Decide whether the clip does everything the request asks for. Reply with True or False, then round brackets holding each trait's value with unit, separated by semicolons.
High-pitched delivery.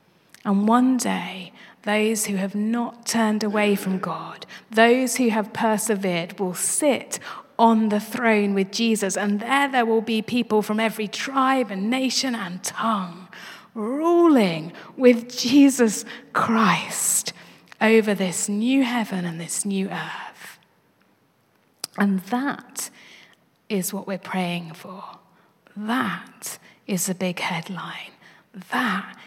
True (215 Hz)